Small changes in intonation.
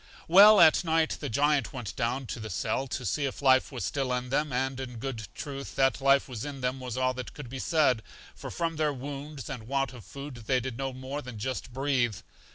Yes: narrow, 2.2 semitones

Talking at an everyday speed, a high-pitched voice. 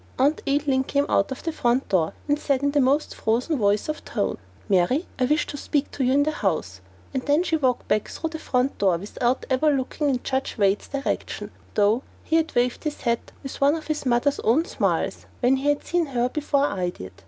No: fast, 220 wpm; very high, 265 Hz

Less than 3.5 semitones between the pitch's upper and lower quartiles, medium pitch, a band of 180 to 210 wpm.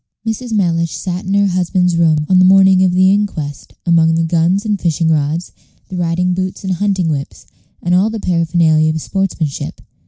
Yes: narrow, 2.6 semitones; medium, 180 Hz; average, 185 wpm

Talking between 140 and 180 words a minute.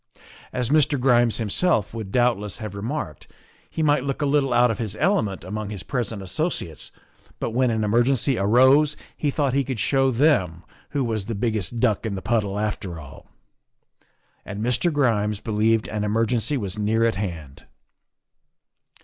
Yes: average, 165 wpm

